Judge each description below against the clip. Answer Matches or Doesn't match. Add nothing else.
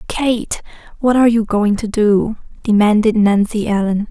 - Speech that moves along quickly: Doesn't match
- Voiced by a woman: Matches